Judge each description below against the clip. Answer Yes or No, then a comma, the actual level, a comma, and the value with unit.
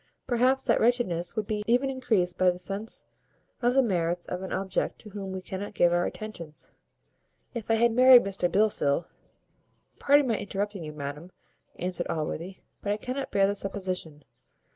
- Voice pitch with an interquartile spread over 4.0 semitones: Yes, average, 4.6 semitones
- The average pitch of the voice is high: Yes, high, 195 Hz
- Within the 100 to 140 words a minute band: No, average, 175 wpm